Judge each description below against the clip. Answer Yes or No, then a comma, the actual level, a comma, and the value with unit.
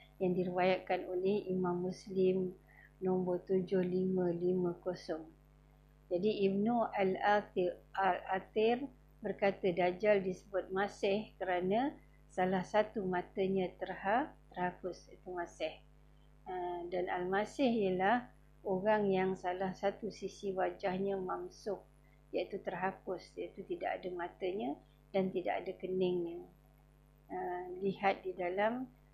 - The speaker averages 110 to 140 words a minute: No, average, 95 wpm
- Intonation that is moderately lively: No, narrow, 1.6 semitones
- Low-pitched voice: No, medium, 185 Hz